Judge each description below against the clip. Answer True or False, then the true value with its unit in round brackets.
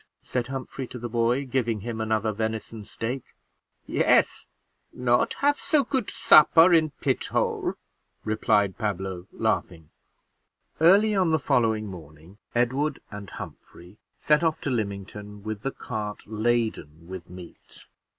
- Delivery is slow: True (130 wpm)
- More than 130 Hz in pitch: False (110 Hz)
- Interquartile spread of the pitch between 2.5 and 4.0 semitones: False (4.7 semitones)